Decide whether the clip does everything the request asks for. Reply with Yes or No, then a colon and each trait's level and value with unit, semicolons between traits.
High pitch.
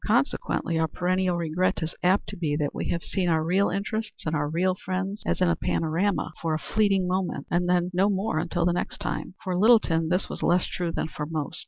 No: medium, 180 Hz